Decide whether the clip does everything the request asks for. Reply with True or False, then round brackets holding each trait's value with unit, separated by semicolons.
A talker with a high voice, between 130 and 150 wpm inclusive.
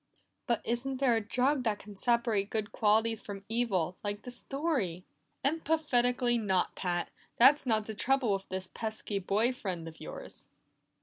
False (225 Hz; 160 wpm)